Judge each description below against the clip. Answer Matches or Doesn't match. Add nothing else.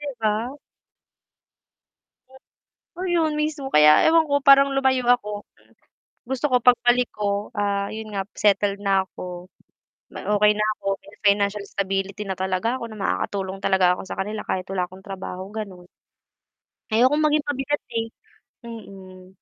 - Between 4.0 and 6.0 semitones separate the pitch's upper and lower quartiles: Matches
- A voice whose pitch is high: Matches